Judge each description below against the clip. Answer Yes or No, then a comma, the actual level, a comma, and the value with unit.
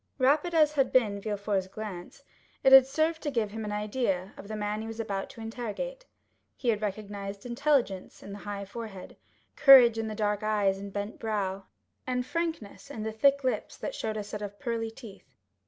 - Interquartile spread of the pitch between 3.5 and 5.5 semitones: Yes, average, 4.2 semitones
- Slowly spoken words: No, average, 195 wpm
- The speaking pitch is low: No, high, 220 Hz